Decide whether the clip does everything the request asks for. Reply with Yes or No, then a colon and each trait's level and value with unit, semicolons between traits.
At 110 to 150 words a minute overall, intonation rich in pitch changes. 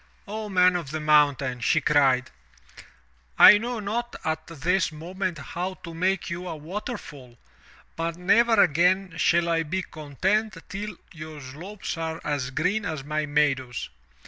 No: average, 145 wpm; average, 4.1 semitones